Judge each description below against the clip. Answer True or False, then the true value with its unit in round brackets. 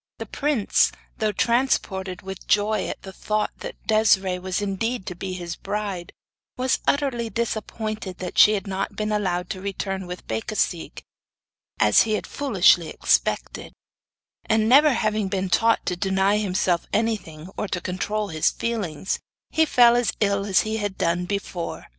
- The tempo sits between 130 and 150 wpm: False (160 wpm)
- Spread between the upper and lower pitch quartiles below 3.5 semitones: True (2.9 semitones)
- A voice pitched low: False (200 Hz)